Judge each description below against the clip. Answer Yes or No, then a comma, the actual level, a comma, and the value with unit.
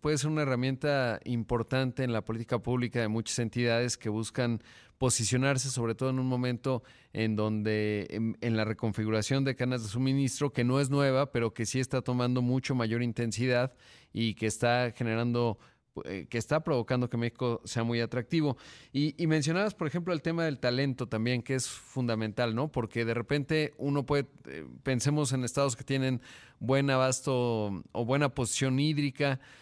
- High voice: No, low, 125 Hz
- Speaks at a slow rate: No, average, 175 wpm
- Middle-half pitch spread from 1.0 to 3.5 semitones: Yes, average, 2.7 semitones